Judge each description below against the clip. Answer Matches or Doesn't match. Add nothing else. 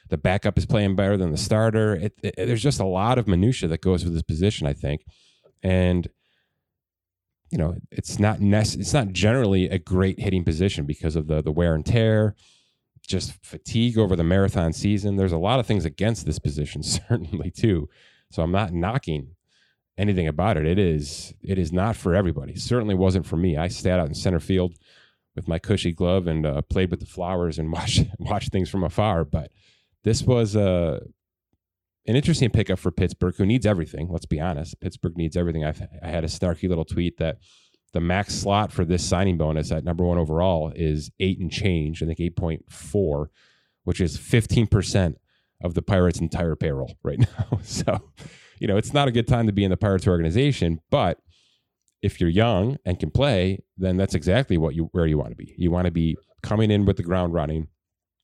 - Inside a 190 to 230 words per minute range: Matches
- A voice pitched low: Matches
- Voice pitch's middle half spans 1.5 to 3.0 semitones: Doesn't match